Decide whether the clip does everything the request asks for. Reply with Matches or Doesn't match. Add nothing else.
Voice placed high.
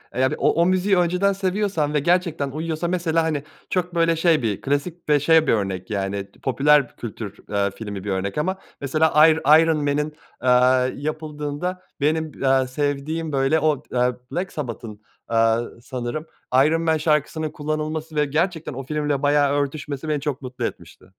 Doesn't match